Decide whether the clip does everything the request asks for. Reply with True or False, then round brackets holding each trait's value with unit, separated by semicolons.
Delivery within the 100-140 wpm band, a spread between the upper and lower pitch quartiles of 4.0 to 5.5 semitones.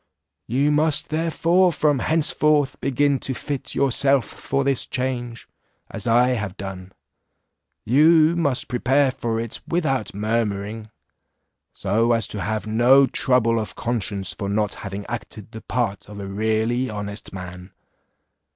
True (135 wpm; 4.7 semitones)